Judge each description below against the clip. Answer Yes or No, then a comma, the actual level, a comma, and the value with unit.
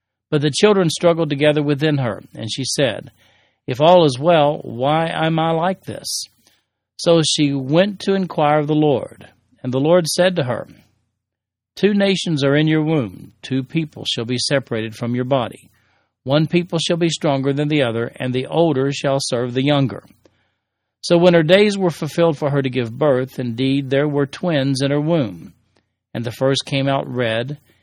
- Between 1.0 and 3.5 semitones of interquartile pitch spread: No, average, 4.6 semitones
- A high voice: No, medium, 140 Hz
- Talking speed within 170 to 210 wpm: Yes, average, 185 wpm